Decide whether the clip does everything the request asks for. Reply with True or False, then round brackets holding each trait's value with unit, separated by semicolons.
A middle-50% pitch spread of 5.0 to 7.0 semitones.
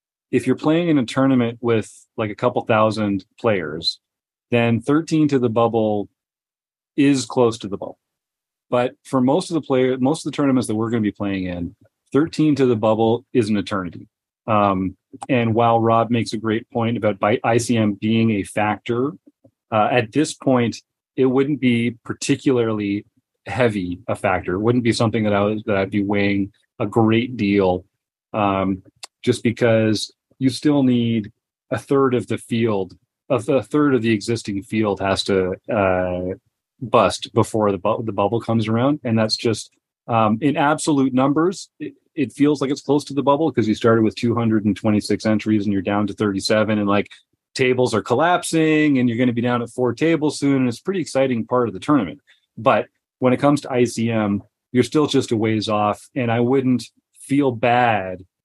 False (3.9 semitones)